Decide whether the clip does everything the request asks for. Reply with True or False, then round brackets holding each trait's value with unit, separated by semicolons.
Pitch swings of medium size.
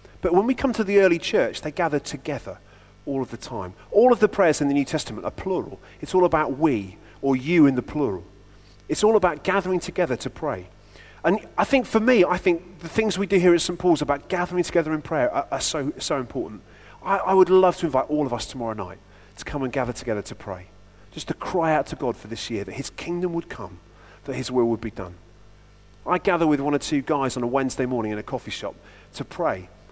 False (8.6 semitones)